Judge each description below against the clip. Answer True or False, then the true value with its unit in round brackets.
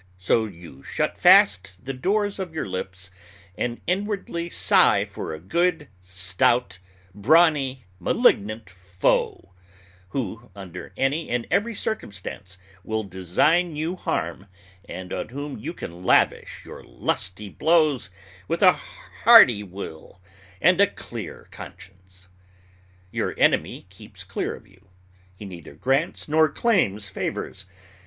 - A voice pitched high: False (110 Hz)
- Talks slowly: True (125 wpm)